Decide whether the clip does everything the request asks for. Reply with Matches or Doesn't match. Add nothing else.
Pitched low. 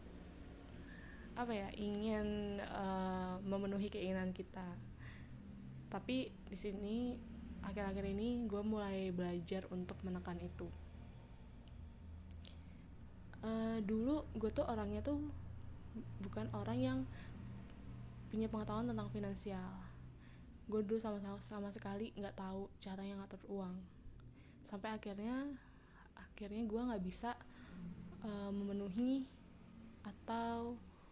Doesn't match